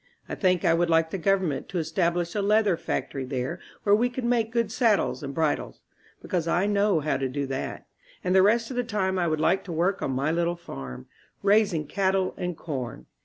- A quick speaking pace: Yes, fast, 220 wpm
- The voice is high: No, medium, 180 Hz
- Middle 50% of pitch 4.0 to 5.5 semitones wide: Yes, average, 4.5 semitones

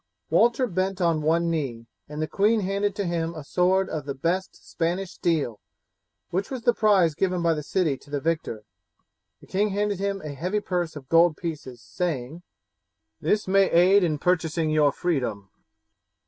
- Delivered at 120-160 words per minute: No, average, 175 wpm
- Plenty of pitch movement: No, average, 3.9 semitones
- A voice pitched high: No, medium, 170 Hz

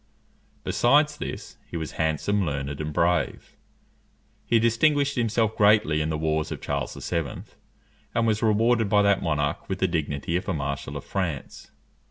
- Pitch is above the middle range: No, very low, 90 Hz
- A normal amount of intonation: No, wide, 6.5 semitones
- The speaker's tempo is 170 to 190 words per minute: No, average, 160 wpm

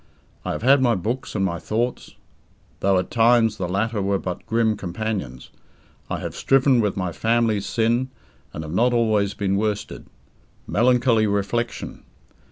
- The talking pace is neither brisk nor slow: Yes, average, 155 wpm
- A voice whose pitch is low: Yes, low, 110 Hz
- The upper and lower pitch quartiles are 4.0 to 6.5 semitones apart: No, average, 3.2 semitones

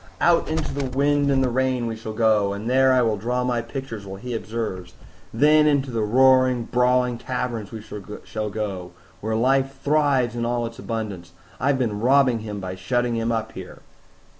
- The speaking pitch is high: No, low, 120 Hz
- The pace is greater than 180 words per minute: Yes, average, 190 wpm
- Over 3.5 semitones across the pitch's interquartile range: No, average, 3.2 semitones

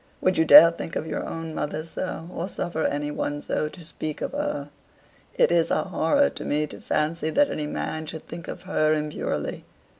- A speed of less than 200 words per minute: No, fast, 205 wpm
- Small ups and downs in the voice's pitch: Yes, narrow, 2.0 semitones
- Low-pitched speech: No, medium, 160 Hz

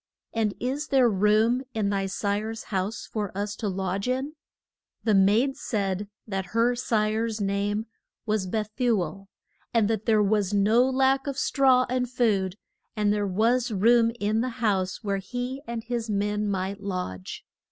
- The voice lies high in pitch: Yes, high, 215 Hz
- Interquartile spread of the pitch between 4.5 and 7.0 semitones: No, average, 3.3 semitones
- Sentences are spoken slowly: No, average, 165 wpm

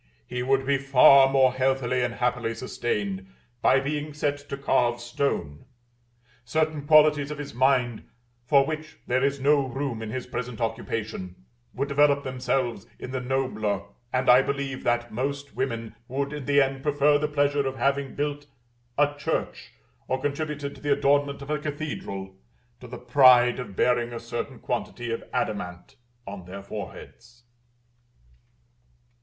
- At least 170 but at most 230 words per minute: No, average, 155 wpm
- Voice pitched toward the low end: Yes, low, 130 Hz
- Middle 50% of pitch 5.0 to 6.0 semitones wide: No, average, 2.9 semitones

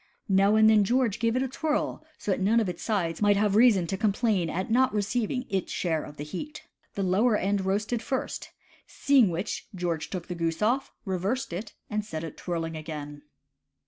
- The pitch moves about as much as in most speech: Yes, average, 4.6 semitones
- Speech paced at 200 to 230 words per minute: Yes, fast, 205 wpm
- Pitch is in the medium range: No, high, 200 Hz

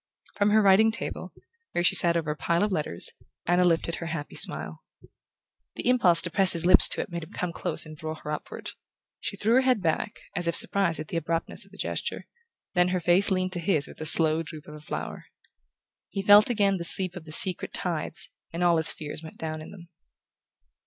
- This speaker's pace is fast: Yes, fast, 220 wpm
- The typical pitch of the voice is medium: Yes, medium, 170 Hz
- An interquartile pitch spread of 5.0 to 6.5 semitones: No, average, 3.2 semitones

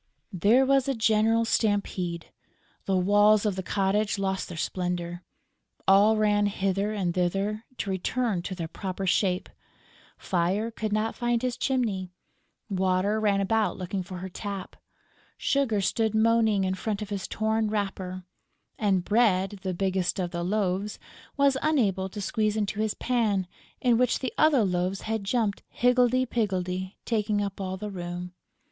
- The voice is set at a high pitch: Yes, high, 205 Hz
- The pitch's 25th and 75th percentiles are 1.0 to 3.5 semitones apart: Yes, average, 2.8 semitones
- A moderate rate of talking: Yes, average, 155 wpm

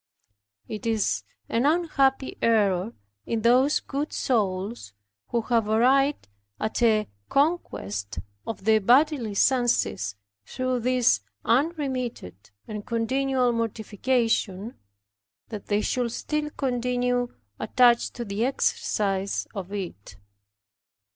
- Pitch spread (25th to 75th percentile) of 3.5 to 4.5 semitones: Yes, average, 3.8 semitones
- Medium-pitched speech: No, high, 235 Hz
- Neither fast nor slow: No, slow, 100 wpm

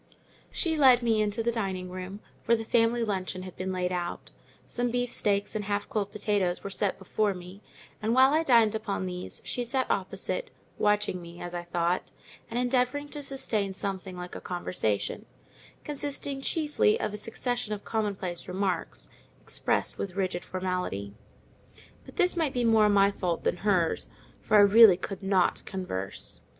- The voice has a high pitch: Yes, high, 205 Hz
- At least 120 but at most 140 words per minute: No, average, 165 wpm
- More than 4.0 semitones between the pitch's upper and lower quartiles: Yes, average, 4.4 semitones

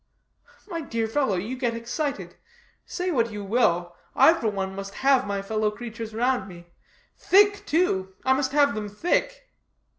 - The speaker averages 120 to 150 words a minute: No, average, 160 wpm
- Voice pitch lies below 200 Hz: No, high, 230 Hz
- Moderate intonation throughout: No, wide, 6.0 semitones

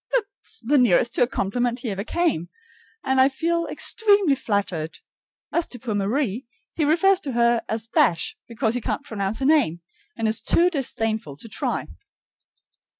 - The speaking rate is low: No, average, 165 wpm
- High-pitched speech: Yes, high, 240 Hz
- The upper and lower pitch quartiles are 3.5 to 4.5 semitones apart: No, wide, 5.6 semitones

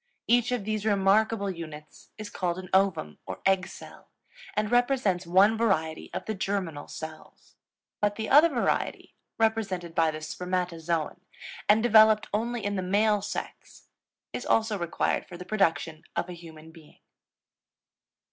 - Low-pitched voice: No, high, 195 Hz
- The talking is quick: No, average, 145 wpm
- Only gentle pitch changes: No, average, 4.3 semitones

